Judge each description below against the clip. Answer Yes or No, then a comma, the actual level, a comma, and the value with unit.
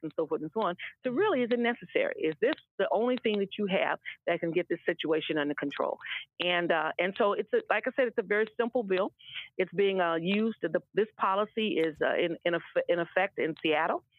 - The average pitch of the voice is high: Yes, high, 195 Hz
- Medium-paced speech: No, fast, 235 wpm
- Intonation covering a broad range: Yes, wide, 6.2 semitones